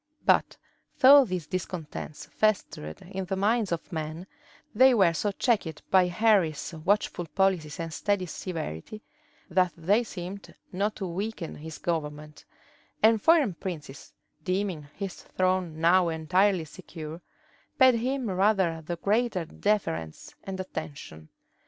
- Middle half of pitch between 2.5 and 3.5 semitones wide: No, average, 4.1 semitones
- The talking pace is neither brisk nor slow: No, slow, 125 wpm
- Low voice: No, medium, 185 Hz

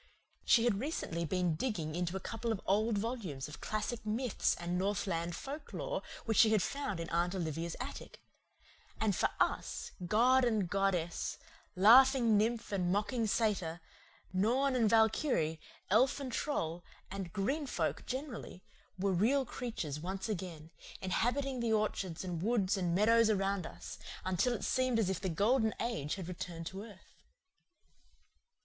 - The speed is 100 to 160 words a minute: Yes, average, 150 wpm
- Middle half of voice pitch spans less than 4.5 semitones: No, average, 4.9 semitones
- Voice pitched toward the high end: Yes, high, 205 Hz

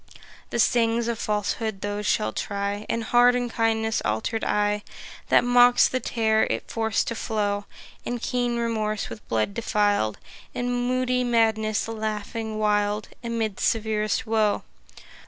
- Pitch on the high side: Yes, high, 220 Hz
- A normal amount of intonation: No, narrow, 2.2 semitones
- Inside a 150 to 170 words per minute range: No, slow, 135 wpm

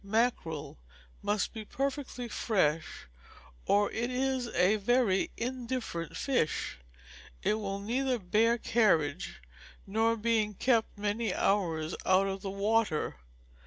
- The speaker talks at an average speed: No, slow, 115 wpm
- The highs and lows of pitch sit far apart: No, average, 3.6 semitones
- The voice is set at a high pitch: Yes, high, 215 Hz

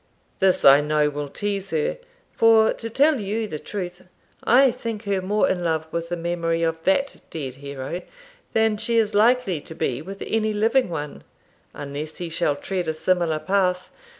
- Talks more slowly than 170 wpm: No, average, 175 wpm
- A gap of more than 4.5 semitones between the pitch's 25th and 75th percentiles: Yes, wide, 5.5 semitones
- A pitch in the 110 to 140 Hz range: No, medium, 185 Hz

